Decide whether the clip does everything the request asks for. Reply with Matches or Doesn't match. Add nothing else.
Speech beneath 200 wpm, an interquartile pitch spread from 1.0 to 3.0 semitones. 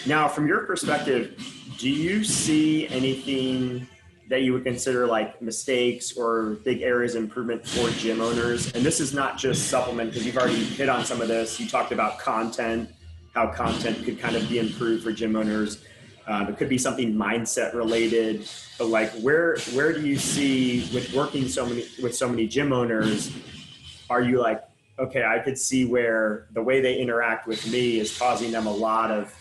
Matches